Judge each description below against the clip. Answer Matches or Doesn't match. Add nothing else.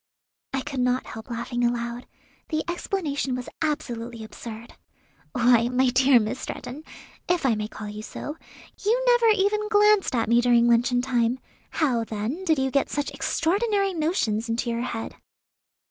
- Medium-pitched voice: Doesn't match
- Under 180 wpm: Matches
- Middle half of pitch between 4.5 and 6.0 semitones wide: Matches